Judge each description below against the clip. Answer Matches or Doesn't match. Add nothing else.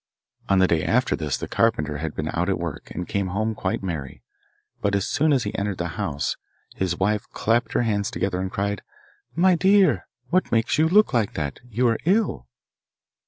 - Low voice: Matches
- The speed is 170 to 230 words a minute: Matches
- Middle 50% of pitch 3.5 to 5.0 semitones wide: Doesn't match